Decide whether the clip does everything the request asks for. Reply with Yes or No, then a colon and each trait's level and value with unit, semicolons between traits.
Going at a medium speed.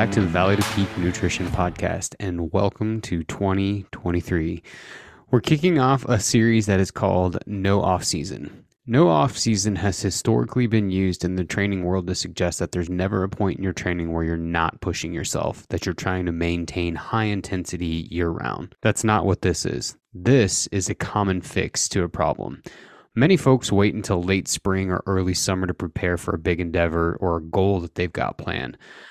Yes: average, 190 wpm